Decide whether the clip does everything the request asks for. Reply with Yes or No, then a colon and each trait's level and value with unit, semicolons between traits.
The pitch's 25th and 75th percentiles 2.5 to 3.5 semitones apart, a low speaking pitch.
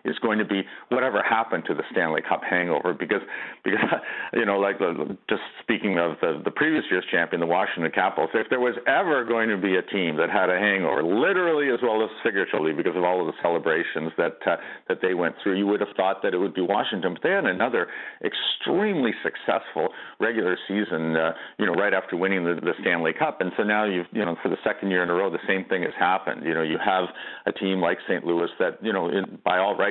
Yes: average, 2.9 semitones; very low, 95 Hz